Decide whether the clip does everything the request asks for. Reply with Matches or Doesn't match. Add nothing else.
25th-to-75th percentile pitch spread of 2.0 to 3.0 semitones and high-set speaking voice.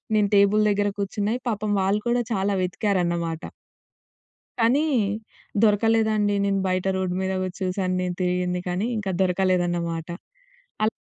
Matches